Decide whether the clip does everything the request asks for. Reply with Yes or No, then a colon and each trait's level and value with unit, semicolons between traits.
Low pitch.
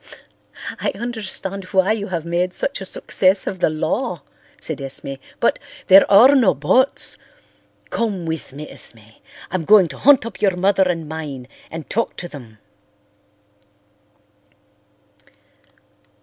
No: medium, 185 Hz